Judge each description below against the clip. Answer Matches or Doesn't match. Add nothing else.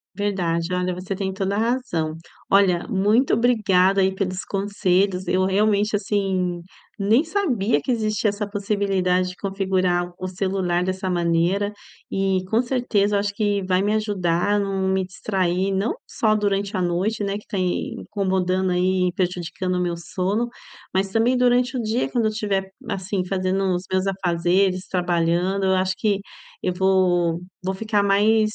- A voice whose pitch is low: Doesn't match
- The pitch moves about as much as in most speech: Doesn't match